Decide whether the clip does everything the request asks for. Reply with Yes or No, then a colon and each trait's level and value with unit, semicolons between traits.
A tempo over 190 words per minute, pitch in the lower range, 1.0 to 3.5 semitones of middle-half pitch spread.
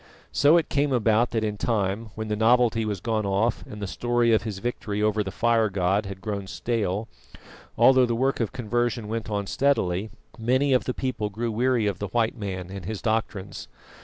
Yes: average, 200 wpm; low, 110 Hz; average, 2.9 semitones